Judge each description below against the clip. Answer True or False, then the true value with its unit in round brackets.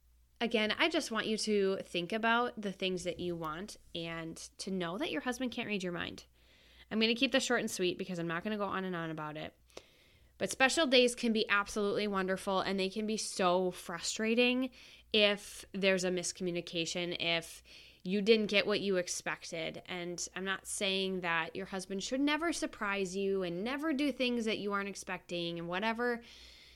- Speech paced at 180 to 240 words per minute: True (195 wpm)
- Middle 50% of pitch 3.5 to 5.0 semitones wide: True (4.2 semitones)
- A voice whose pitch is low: False (195 Hz)